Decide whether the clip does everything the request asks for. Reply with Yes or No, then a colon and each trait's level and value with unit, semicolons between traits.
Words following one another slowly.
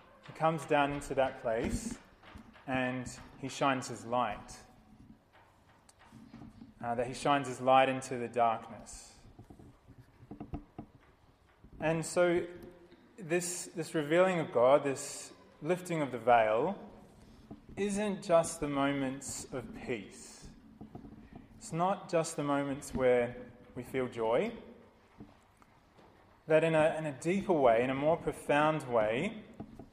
Yes: slow, 120 wpm